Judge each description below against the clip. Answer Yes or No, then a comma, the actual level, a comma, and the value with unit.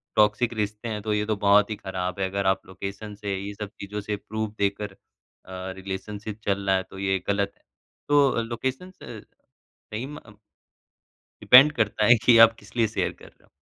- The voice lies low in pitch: Yes, low, 105 Hz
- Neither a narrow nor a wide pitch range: No, narrow, 2.1 semitones